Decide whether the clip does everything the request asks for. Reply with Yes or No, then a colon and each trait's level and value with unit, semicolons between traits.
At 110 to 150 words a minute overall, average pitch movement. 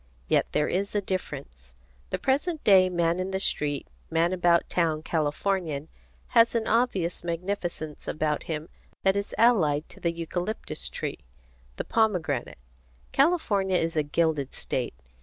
Yes: average, 140 wpm; average, 4.4 semitones